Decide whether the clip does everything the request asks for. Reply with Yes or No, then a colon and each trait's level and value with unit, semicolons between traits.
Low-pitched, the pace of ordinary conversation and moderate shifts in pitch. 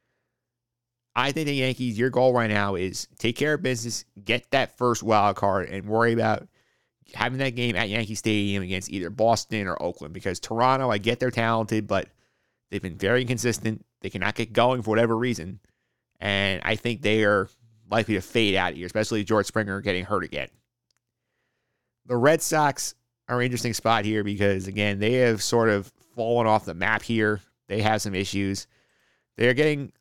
Yes: low, 110 Hz; average, 180 wpm; average, 3.1 semitones